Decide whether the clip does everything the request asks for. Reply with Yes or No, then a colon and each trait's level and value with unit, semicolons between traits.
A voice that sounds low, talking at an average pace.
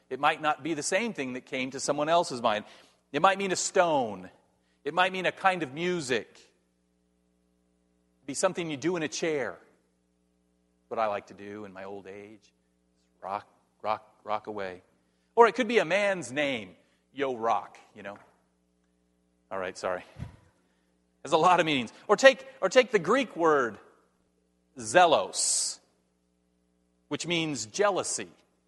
Yes: low, 100 Hz; average, 160 wpm